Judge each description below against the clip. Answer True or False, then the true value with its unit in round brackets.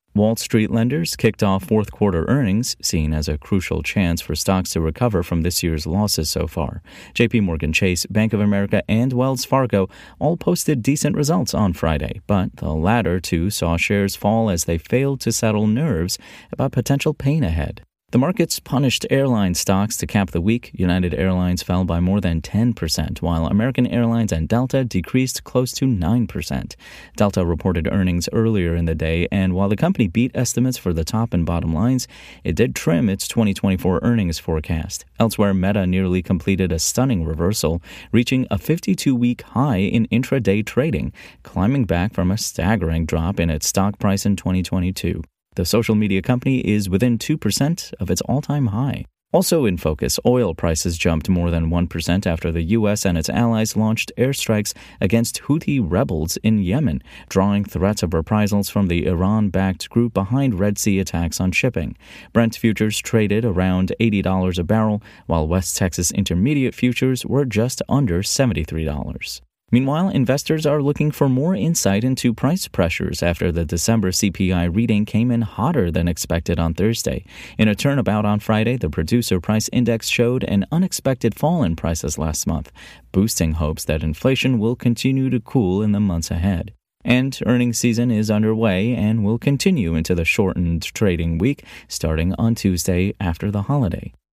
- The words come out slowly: False (170 wpm)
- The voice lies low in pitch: True (100 Hz)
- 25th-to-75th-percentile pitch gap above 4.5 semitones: True (5.3 semitones)